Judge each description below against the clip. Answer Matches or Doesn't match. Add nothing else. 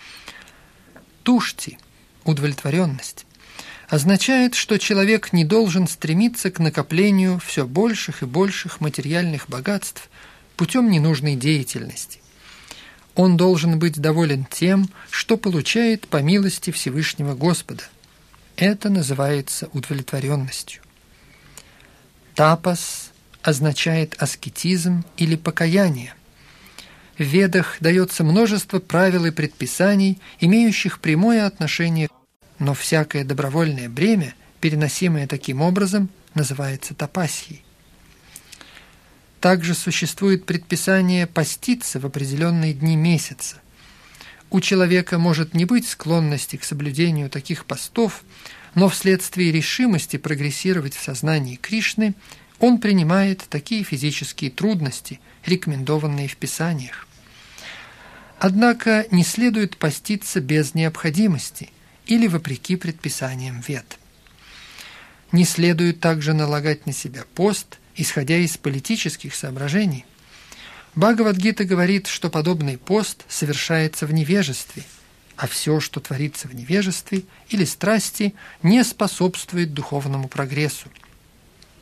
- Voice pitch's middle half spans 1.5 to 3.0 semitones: Doesn't match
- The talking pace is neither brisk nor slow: Doesn't match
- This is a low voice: Doesn't match